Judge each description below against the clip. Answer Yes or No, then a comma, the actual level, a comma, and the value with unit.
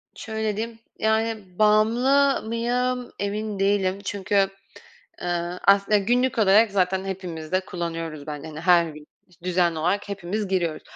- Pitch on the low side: No, high, 195 Hz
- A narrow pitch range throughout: No, average, 3.8 semitones